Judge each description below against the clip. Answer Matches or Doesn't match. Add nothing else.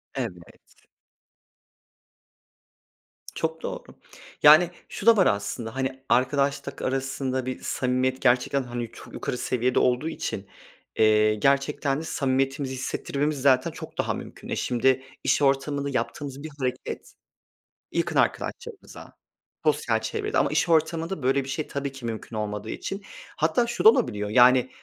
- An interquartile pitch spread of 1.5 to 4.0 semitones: Matches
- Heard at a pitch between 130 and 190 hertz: Matches